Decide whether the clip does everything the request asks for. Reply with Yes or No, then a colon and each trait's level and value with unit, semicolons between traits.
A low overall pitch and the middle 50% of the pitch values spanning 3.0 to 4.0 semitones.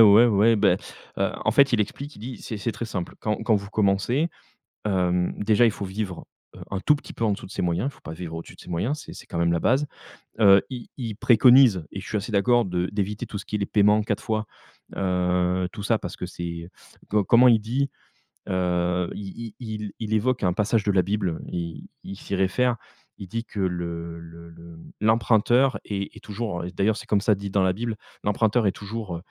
Yes: low, 100 Hz; average, 3.7 semitones